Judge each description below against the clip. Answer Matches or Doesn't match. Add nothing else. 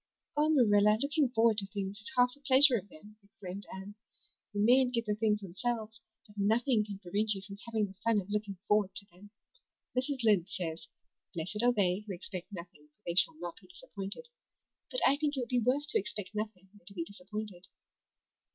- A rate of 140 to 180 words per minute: Doesn't match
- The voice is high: Matches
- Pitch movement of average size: Matches